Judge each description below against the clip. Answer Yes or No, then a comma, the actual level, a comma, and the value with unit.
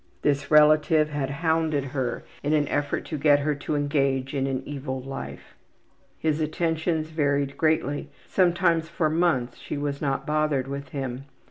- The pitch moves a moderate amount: No, narrow, 2.3 semitones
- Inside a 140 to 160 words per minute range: Yes, average, 155 wpm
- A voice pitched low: No, medium, 145 Hz